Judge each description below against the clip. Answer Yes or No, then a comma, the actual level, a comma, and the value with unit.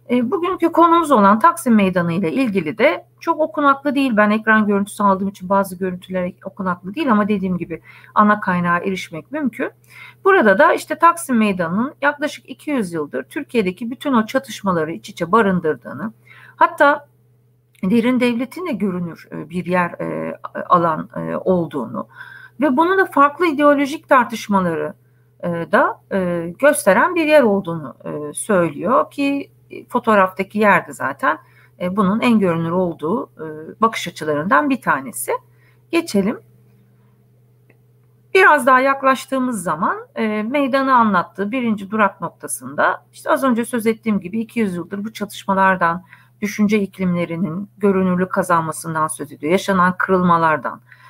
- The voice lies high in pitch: Yes, high, 200 Hz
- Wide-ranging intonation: Yes, wide, 7.4 semitones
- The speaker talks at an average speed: Yes, average, 120 wpm